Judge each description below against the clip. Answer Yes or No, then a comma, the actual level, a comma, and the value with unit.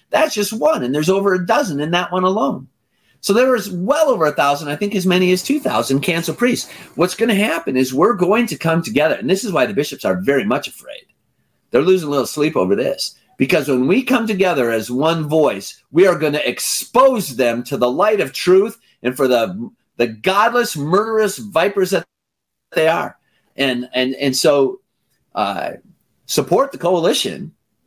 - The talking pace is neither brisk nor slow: No, fast, 195 wpm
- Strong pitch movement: Yes, wide, 7.1 semitones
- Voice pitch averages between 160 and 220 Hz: Yes, medium, 185 Hz